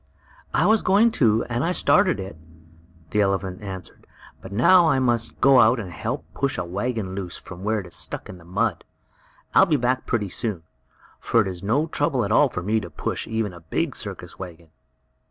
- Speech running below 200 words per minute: No, fast, 205 wpm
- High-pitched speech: No, low, 110 Hz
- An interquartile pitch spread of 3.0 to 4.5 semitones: No, wide, 5.5 semitones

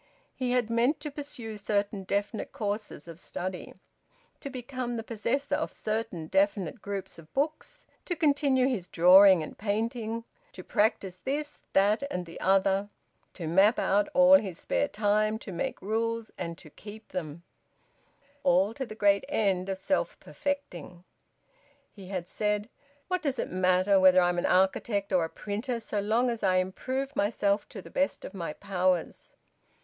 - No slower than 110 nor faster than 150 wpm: No, average, 165 wpm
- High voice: Yes, high, 205 Hz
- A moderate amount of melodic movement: Yes, average, 4.6 semitones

